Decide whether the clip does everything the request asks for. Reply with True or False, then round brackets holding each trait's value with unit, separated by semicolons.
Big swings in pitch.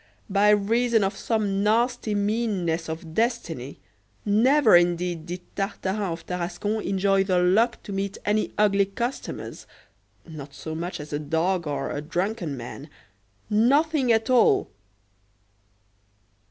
False (4.3 semitones)